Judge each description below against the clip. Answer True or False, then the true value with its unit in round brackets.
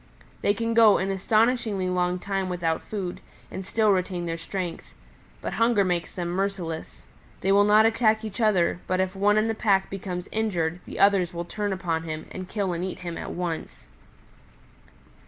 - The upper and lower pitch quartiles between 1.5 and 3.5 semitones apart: True (2.9 semitones)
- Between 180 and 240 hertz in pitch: True (190 Hz)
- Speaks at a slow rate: False (180 wpm)